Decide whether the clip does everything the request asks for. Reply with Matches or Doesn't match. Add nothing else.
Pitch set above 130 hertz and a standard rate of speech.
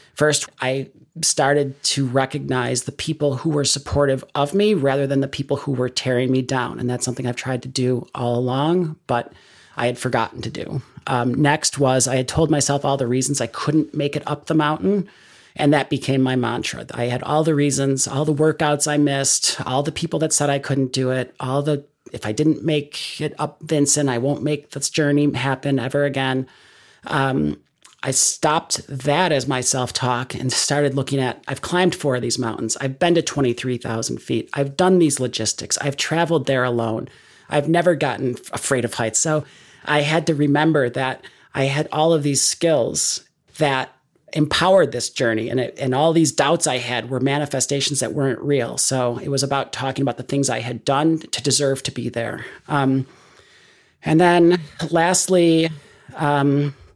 Matches